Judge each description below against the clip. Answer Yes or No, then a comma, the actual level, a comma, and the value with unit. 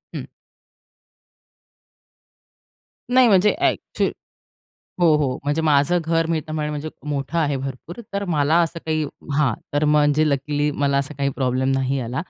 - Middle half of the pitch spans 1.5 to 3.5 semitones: Yes, average, 2.8 semitones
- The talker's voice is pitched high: No, medium, 150 Hz